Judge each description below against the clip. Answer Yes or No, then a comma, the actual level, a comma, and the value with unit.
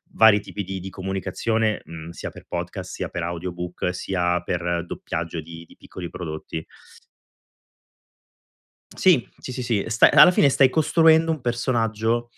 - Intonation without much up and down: No, wide, 5.4 semitones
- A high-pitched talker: No, very low, 95 Hz